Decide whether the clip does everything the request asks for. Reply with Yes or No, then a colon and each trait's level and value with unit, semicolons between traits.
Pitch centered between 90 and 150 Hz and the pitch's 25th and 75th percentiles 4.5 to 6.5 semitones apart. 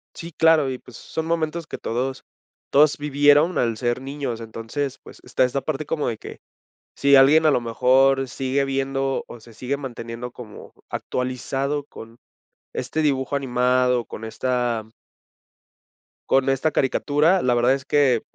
No: low, 135 Hz; average, 2.8 semitones